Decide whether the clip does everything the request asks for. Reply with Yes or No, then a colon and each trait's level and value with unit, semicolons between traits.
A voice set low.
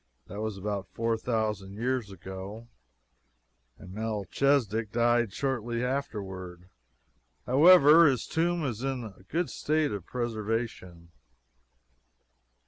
Yes: low, 115 Hz